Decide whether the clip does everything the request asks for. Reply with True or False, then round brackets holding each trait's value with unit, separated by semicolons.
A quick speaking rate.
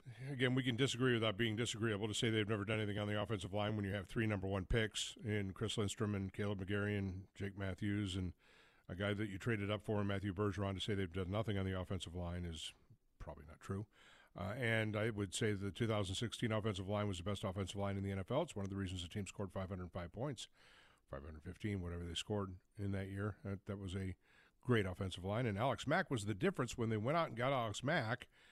True (235 wpm)